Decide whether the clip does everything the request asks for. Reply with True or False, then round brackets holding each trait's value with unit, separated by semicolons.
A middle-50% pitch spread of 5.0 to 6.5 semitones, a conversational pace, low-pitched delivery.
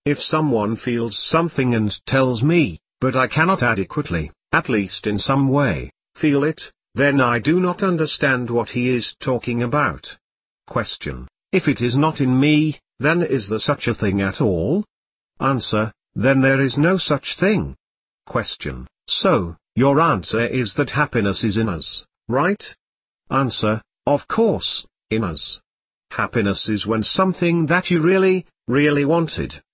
True (5.6 semitones; 150 wpm; 130 Hz)